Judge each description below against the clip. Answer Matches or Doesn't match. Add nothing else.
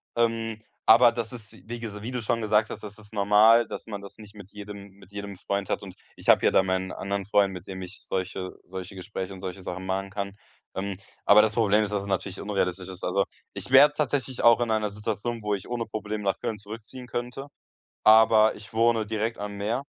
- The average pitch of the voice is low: Matches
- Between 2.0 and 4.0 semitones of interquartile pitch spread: Matches